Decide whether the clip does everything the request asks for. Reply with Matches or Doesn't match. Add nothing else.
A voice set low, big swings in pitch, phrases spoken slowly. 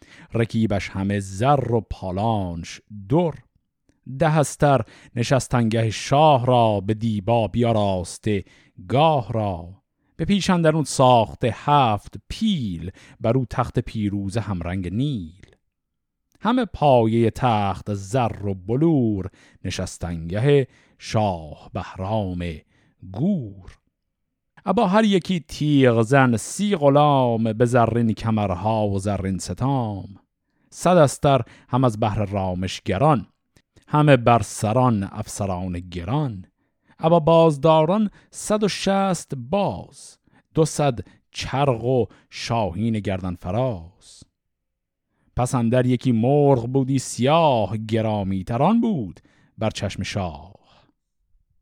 Matches